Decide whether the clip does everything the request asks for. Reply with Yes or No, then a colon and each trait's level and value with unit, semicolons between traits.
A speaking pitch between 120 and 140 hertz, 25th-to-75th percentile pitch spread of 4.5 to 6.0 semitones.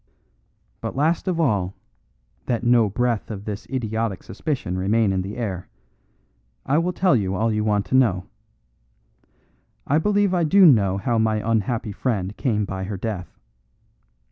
No: low, 110 Hz; average, 4.8 semitones